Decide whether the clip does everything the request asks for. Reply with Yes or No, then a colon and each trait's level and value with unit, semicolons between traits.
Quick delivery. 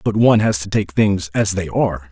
Yes: fast, 255 wpm